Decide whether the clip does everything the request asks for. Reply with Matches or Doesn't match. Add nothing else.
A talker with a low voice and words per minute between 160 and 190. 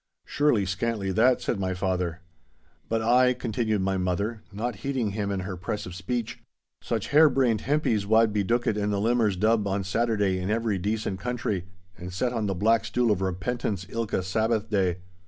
Matches